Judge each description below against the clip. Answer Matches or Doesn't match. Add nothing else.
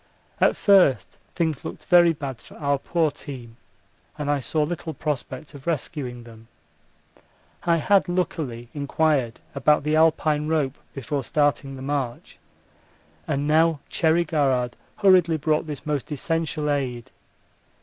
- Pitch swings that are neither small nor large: Matches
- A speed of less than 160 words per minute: Matches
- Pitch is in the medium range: Matches